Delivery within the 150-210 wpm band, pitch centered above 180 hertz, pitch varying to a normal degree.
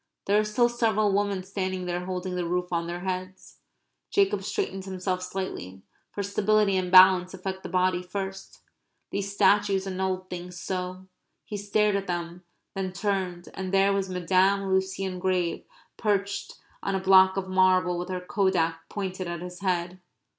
No: average, 160 wpm; high, 190 Hz; narrow, 1.5 semitones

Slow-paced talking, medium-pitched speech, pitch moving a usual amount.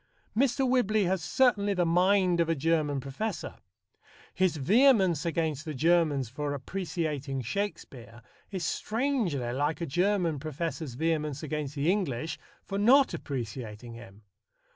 No: slow, 130 wpm; medium, 160 Hz; wide, 5.8 semitones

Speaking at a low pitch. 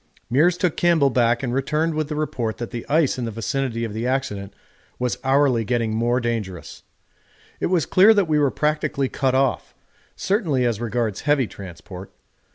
Yes: low, 130 Hz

